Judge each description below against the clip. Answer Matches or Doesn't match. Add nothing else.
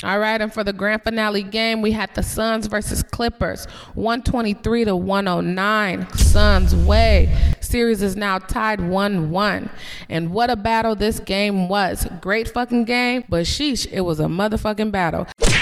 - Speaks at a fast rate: Doesn't match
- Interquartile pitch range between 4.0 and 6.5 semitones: Doesn't match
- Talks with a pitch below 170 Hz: Doesn't match